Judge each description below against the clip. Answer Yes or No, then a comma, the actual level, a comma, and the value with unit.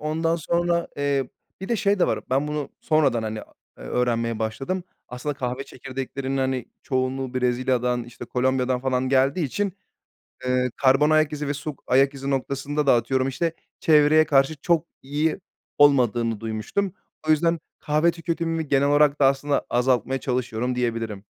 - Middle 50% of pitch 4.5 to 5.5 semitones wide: No, average, 3.3 semitones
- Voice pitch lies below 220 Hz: Yes, low, 135 Hz